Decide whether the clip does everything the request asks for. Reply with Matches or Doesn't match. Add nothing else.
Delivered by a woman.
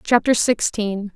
Matches